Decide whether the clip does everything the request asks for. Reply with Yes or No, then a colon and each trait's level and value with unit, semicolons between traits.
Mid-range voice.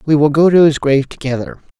Yes: medium, 145 Hz